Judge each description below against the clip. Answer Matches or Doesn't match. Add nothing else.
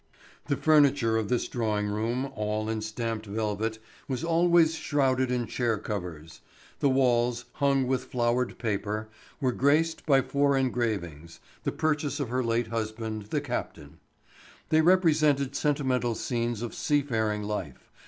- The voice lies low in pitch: Matches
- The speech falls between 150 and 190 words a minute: Doesn't match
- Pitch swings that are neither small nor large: Matches